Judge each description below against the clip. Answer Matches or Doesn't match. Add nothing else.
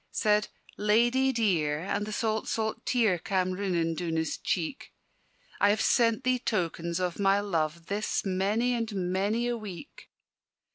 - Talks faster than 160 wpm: Doesn't match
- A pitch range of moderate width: Matches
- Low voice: Doesn't match